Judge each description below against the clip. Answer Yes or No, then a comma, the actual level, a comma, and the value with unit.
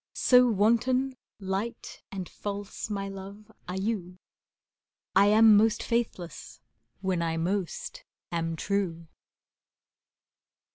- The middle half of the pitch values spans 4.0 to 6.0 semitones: No, average, 3.4 semitones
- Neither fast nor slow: No, slow, 100 wpm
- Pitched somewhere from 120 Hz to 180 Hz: No, high, 200 Hz